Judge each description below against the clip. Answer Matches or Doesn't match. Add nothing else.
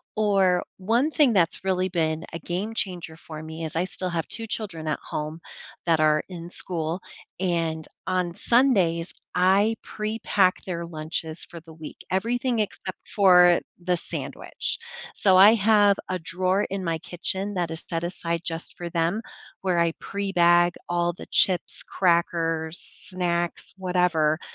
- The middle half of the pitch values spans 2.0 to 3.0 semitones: Matches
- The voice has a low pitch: Doesn't match